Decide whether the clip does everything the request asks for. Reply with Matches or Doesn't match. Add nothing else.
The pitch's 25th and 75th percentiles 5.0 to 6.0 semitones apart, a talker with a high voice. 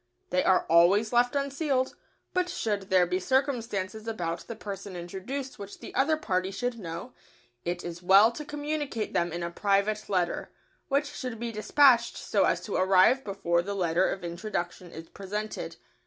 Matches